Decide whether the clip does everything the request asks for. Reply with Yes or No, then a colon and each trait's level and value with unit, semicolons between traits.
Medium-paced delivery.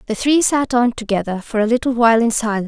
No: fast, 245 wpm